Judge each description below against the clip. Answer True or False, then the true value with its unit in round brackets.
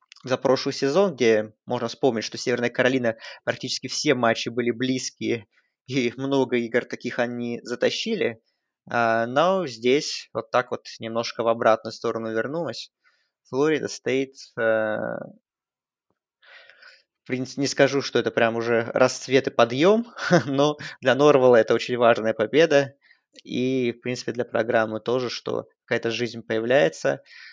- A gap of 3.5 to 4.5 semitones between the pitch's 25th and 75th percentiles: False (2.7 semitones)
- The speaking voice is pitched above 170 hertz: False (125 Hz)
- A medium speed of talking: True (130 wpm)